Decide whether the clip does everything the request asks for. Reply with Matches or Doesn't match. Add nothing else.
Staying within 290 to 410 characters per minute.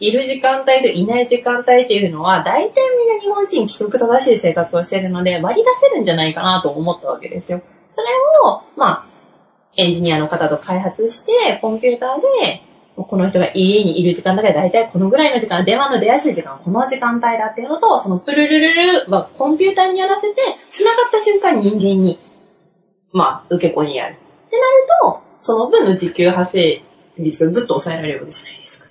Doesn't match